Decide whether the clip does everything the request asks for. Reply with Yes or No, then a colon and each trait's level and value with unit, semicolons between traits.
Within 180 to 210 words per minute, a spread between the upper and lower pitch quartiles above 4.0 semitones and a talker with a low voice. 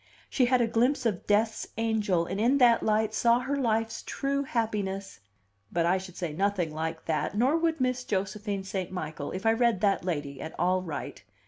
No: average, 195 wpm; average, 4.4 semitones; high, 210 Hz